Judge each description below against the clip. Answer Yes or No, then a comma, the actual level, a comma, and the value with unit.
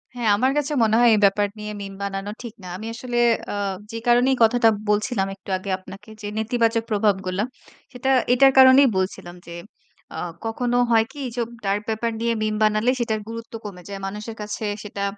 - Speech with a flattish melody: No, average, 3.0 semitones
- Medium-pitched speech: No, high, 220 Hz